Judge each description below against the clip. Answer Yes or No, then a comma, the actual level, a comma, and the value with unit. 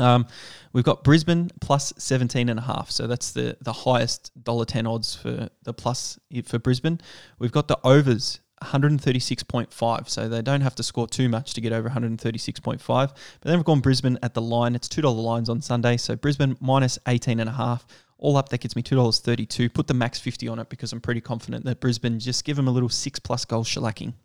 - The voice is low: Yes, low, 125 Hz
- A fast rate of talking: Yes, fast, 250 wpm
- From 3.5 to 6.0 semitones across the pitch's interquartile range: No, narrow, 2.5 semitones